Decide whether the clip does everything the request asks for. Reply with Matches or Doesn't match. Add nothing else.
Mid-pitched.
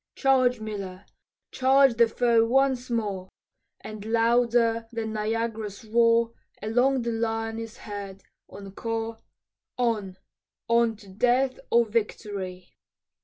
Doesn't match